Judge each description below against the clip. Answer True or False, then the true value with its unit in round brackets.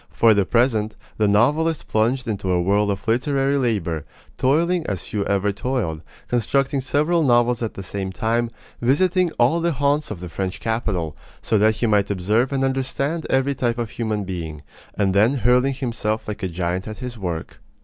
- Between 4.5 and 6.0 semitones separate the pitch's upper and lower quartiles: True (5.1 semitones)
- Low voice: True (115 Hz)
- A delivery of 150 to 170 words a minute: False (180 wpm)